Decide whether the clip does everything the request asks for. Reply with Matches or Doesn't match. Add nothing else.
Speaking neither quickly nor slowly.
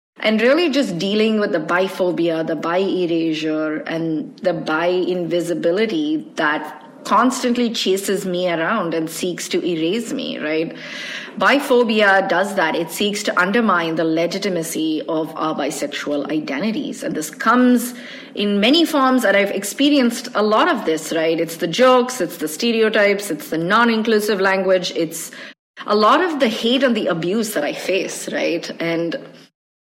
Matches